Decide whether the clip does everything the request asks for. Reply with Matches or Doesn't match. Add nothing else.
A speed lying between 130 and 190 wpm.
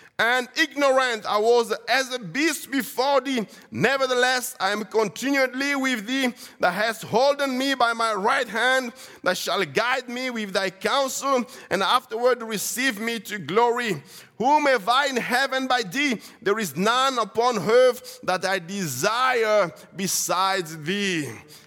Matches